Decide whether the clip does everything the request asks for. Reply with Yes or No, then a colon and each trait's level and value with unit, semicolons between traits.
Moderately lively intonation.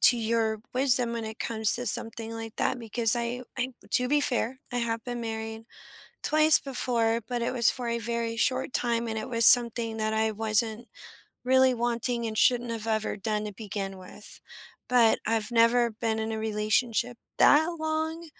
No: narrow, 1.8 semitones